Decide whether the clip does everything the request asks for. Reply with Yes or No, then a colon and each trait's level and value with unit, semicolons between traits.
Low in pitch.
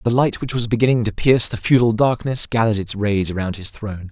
Yes: low, 110 Hz